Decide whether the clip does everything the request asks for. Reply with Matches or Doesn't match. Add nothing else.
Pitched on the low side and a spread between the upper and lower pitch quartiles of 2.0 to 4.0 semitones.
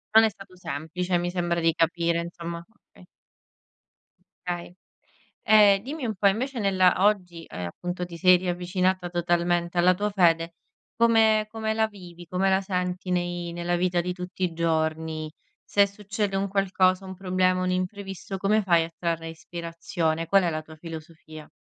Doesn't match